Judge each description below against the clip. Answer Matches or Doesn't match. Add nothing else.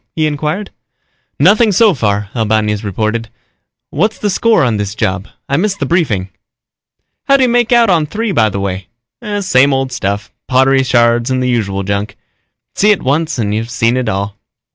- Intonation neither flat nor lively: Doesn't match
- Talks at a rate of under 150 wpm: Doesn't match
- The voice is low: Matches